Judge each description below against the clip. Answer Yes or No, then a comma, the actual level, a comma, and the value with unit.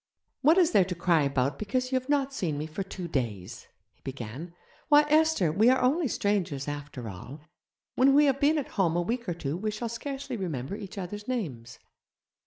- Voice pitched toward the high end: Yes, high, 195 Hz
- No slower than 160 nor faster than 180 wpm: No, average, 200 wpm